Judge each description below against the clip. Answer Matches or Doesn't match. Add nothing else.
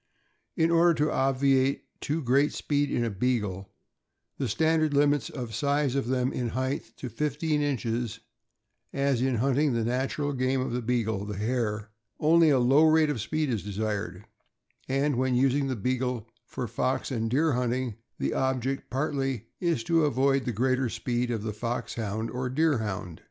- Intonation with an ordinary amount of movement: Matches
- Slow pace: Doesn't match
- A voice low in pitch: Matches